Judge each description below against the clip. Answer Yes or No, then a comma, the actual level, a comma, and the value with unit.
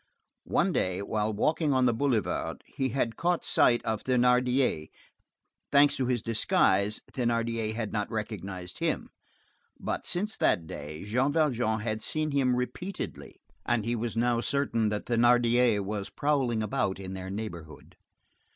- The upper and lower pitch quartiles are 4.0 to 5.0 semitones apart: No, average, 3.4 semitones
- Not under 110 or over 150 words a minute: Yes, average, 145 wpm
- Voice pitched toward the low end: Yes, low, 115 Hz